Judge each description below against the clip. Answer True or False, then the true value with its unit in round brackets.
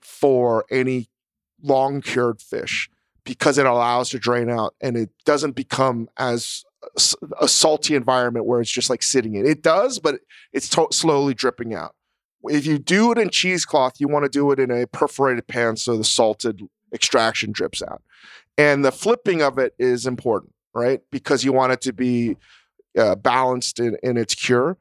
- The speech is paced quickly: False (175 wpm)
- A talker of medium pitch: False (130 Hz)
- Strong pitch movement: False (3.0 semitones)